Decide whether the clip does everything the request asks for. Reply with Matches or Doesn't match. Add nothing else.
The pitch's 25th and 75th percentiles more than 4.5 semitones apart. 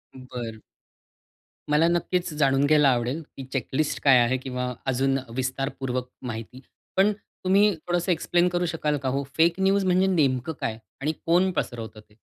Matches